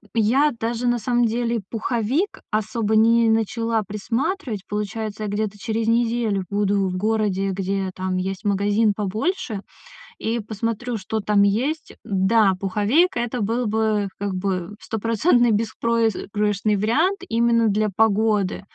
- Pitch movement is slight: Yes, narrow, 2.3 semitones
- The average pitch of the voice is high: Yes, high, 220 Hz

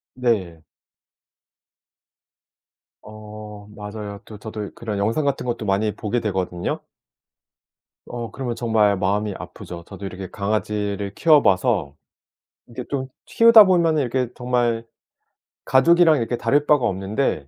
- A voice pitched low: Yes, low, 110 Hz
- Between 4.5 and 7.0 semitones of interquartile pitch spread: No, average, 3.8 semitones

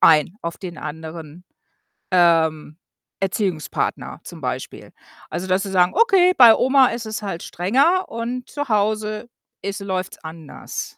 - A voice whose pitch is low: No, high, 195 Hz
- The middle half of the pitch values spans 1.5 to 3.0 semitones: No, wide, 5.6 semitones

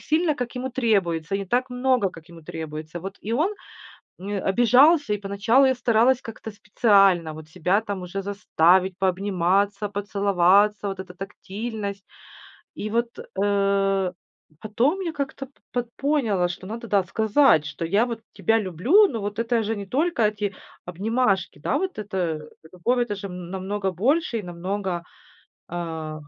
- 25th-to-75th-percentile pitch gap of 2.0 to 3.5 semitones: No, average, 4.1 semitones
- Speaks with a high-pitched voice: Yes, high, 205 Hz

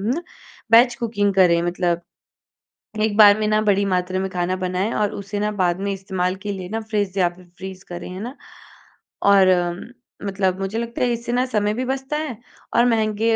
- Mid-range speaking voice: No, high, 200 Hz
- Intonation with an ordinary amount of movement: Yes, average, 3.3 semitones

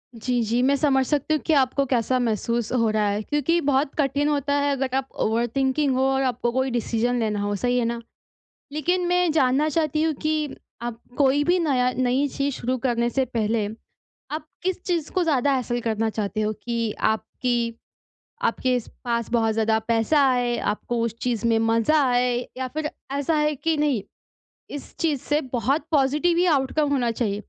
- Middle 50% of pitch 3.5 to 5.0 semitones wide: Yes, average, 4.0 semitones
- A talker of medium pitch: No, very high, 260 Hz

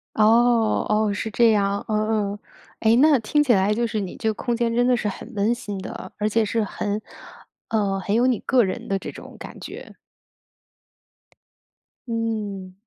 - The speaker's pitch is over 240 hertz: No, high, 220 Hz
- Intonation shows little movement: Yes, narrow, 2.3 semitones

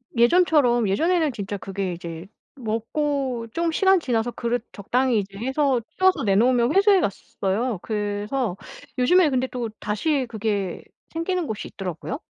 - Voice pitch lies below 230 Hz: No, high, 240 Hz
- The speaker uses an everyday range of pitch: No, wide, 6.2 semitones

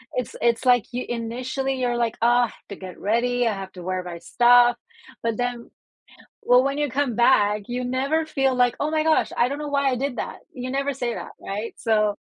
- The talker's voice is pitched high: Yes, high, 245 Hz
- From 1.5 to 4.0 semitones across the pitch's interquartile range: Yes, narrow, 2.5 semitones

